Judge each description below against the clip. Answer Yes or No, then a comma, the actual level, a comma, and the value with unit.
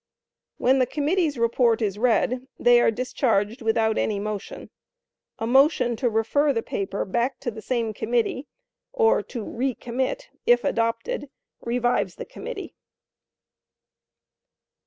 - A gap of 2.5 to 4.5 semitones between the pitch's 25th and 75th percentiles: Yes, average, 2.9 semitones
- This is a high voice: Yes, high, 240 Hz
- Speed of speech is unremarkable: No, slow, 130 wpm